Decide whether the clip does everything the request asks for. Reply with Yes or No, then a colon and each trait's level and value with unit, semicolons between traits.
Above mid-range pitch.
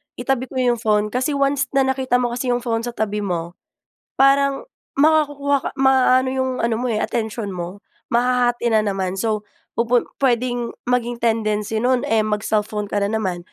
Yes: high, 240 Hz